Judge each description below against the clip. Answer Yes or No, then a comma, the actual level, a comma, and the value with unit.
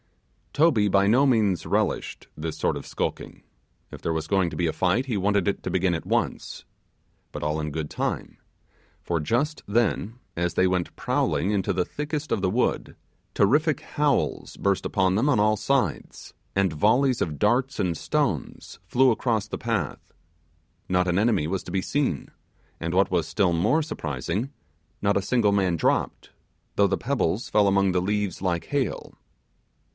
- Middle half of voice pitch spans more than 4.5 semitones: Yes, average, 5.1 semitones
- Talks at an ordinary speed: Yes, average, 175 wpm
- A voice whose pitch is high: No, low, 100 Hz